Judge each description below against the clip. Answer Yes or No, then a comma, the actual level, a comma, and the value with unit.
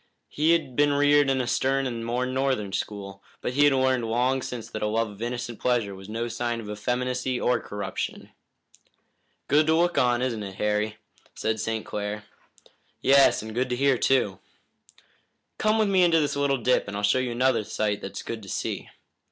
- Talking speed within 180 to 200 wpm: Yes, average, 195 wpm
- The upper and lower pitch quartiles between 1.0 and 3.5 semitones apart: No, average, 3.9 semitones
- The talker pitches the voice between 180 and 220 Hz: No, low, 125 Hz